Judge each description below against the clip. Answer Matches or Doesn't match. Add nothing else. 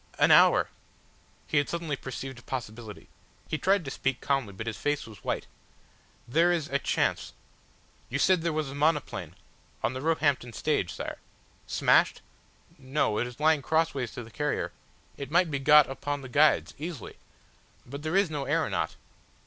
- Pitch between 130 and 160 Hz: Matches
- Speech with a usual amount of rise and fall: Matches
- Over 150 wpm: Matches